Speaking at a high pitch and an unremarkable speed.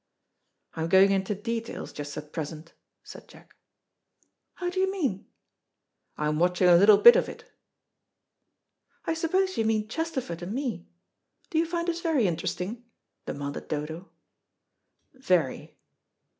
No: high, 205 Hz; slow, 130 wpm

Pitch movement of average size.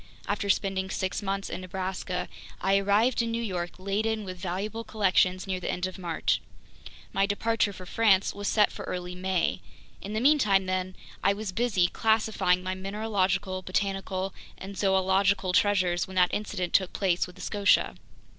No: narrow, 1.8 semitones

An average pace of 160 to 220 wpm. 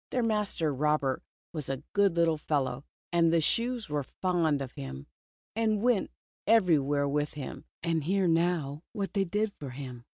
Yes: average, 165 wpm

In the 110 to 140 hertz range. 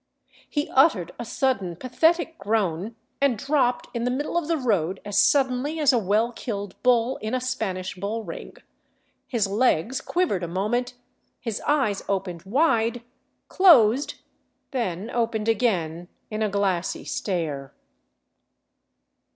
No: high, 225 Hz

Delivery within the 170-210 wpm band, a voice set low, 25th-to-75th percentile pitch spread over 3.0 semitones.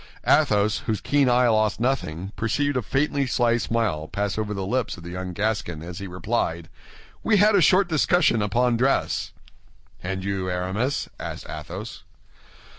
No: average, 160 wpm; low, 110 Hz; wide, 5.6 semitones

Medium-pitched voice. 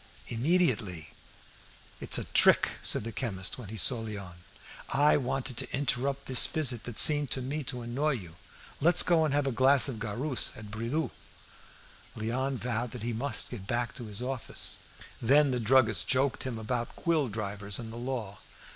No: low, 125 Hz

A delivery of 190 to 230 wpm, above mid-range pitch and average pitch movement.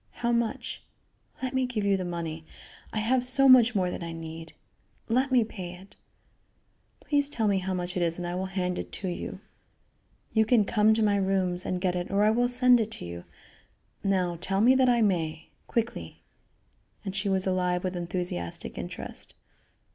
Yes: average, 195 wpm; high, 195 Hz; average, 4.6 semitones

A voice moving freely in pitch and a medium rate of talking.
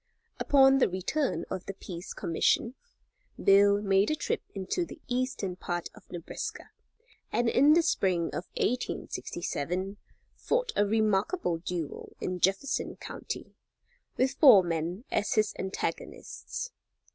No: wide, 6.2 semitones; slow, 125 wpm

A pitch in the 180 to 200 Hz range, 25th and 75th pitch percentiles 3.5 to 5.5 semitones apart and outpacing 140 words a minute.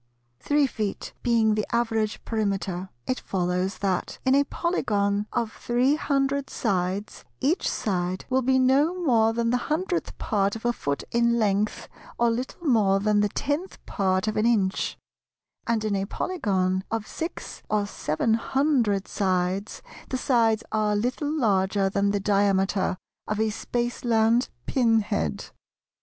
No: high, 220 Hz; average, 3.8 semitones; average, 150 wpm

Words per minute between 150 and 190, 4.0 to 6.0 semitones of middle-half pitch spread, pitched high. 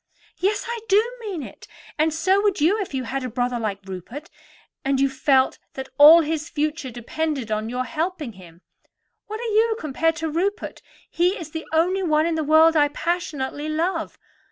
Yes: average, 185 wpm; average, 4.8 semitones; very high, 310 Hz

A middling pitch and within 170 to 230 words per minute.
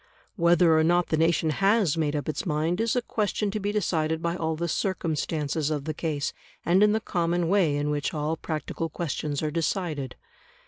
Yes: medium, 165 Hz; average, 195 wpm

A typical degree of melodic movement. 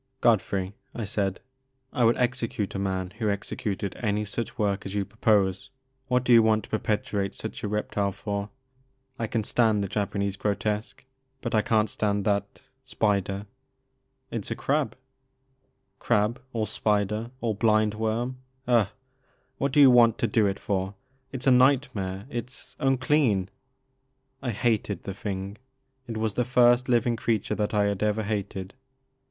Yes: average, 3.3 semitones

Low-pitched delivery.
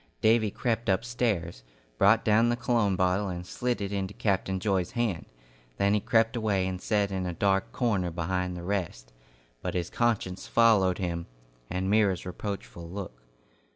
Yes: very low, 95 Hz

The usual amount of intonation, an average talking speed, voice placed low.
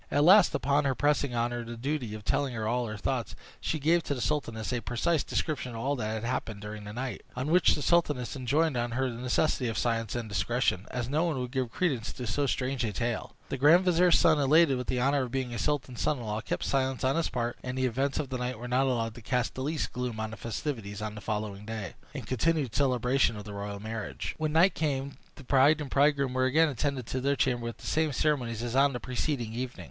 No: average, 3.6 semitones; fast, 255 wpm; low, 125 Hz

